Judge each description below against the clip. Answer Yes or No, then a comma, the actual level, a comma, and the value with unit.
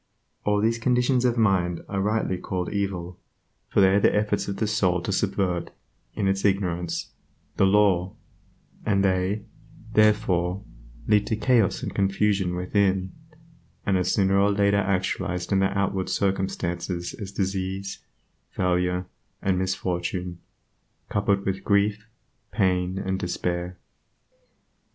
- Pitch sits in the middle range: No, very low, 95 Hz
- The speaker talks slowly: Yes, slow, 130 wpm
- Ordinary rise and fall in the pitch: No, narrow, 1.9 semitones